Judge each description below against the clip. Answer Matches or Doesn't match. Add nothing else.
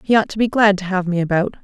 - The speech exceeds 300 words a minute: Matches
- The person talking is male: Doesn't match